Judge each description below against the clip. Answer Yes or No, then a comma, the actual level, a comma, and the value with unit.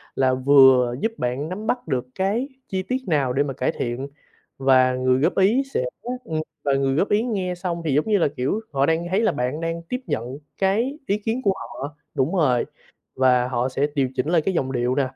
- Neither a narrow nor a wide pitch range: No, wide, 6.8 semitones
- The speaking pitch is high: No, medium, 145 Hz